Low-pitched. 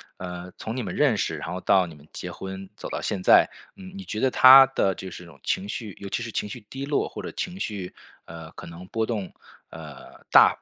Yes: low, 100 Hz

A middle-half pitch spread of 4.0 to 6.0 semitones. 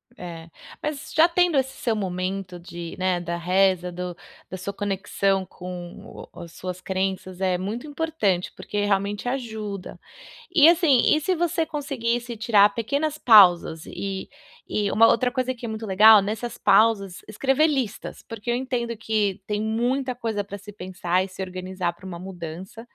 Yes: average, 4.7 semitones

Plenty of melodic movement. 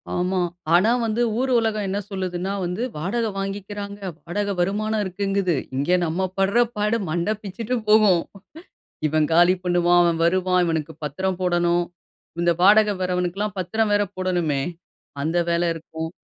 No: average, 2.9 semitones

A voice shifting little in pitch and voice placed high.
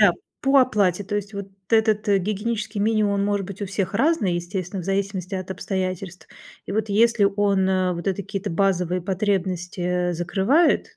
Yes: narrow, 2.2 semitones; high, 200 Hz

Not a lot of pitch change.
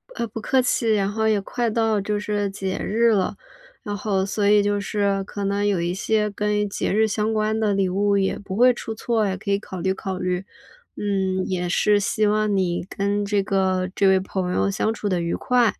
Yes: narrow, 1.9 semitones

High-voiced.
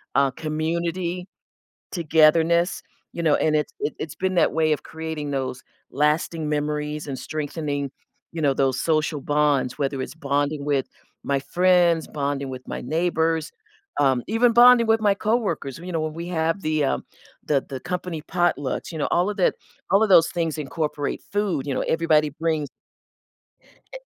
No: medium, 155 Hz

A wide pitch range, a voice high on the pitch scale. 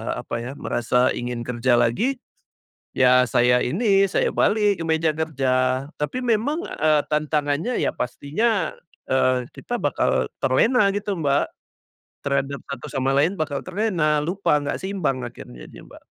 No: wide, 7.1 semitones; medium, 145 Hz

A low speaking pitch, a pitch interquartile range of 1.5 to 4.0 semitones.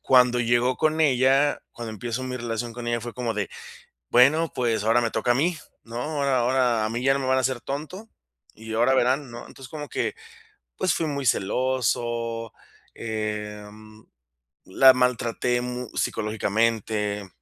Yes: low, 120 Hz; average, 2.7 semitones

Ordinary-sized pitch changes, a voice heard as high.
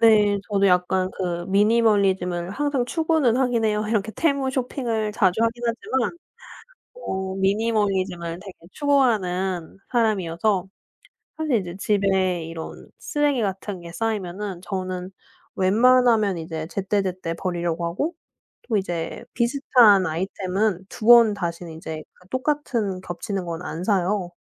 Yes: average, 4.3 semitones; high, 200 Hz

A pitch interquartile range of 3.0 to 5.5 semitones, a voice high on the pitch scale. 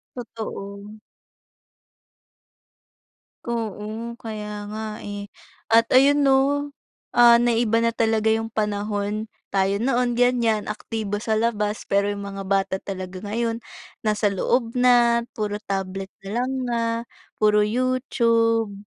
No: narrow, 2.4 semitones; high, 220 Hz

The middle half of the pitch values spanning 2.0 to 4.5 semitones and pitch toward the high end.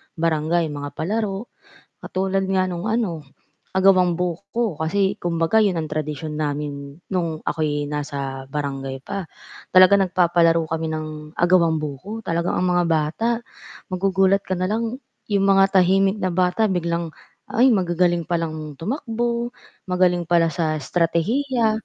No: average, 3.7 semitones; medium, 175 Hz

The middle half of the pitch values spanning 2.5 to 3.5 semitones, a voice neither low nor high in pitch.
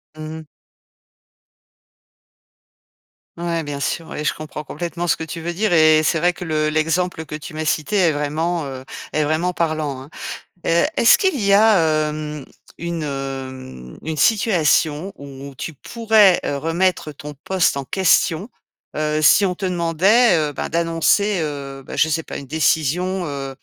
Yes: average, 3.1 semitones; medium, 160 Hz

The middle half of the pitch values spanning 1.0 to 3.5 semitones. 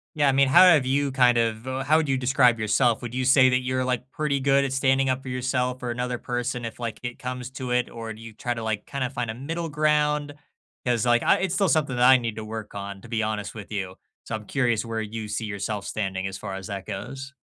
Yes: average, 3.2 semitones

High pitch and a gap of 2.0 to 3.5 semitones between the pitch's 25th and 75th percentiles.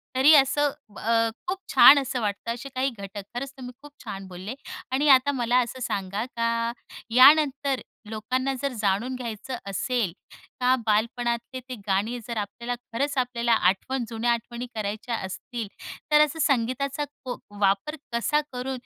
Yes: high, 245 Hz; average, 3.2 semitones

